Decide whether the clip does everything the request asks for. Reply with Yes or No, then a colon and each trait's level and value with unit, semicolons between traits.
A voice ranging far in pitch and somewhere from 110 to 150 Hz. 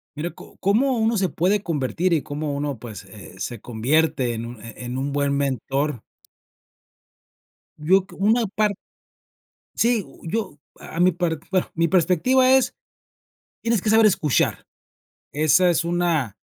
No: wide, 6.0 semitones; medium, 160 Hz